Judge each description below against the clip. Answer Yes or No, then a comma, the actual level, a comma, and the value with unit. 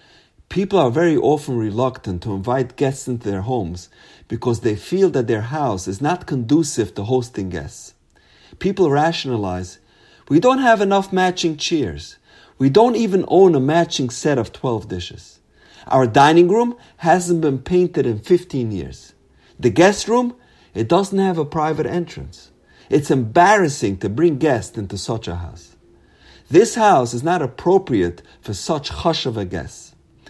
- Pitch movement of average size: No, wide, 8.6 semitones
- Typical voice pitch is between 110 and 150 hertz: Yes, low, 135 Hz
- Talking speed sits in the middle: Yes, average, 155 wpm